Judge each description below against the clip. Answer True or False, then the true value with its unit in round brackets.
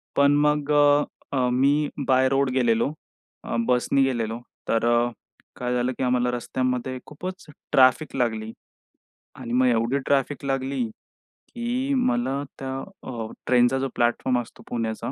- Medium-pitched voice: False (130 Hz)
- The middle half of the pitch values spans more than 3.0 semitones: False (2.7 semitones)